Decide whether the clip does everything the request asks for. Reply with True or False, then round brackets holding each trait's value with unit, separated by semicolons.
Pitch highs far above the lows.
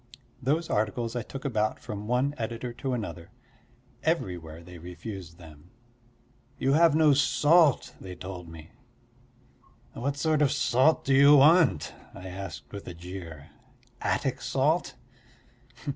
True (7.8 semitones)